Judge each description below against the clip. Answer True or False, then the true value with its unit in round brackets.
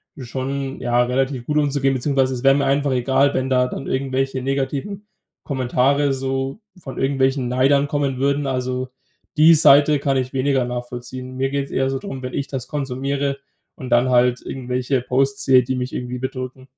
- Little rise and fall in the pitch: True (1.4 semitones)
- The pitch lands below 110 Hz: False (135 Hz)